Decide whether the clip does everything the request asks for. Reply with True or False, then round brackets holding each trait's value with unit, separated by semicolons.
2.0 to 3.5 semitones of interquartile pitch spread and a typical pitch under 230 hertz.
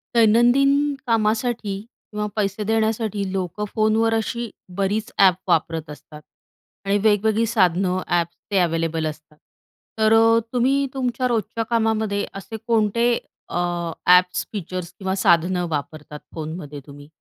False (4.4 semitones; 205 Hz)